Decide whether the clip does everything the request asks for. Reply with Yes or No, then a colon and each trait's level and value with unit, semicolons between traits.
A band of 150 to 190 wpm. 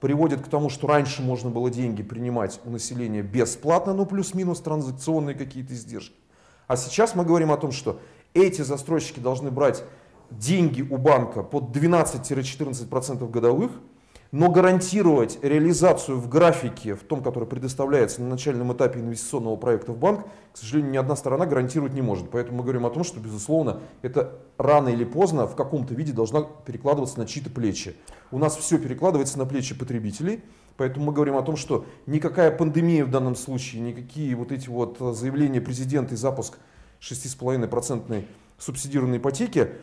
Yes: fast, 160 wpm